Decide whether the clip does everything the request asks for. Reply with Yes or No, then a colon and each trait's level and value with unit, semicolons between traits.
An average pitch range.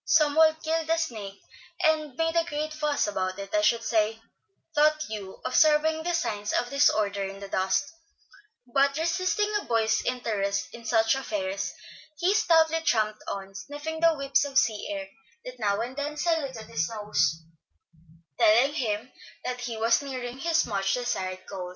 No: wide, 6.6 semitones